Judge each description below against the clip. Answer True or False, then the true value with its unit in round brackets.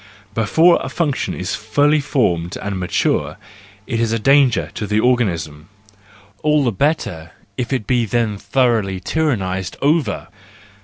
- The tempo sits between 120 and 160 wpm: True (140 wpm)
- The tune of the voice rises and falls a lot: True (6.2 semitones)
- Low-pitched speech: True (115 Hz)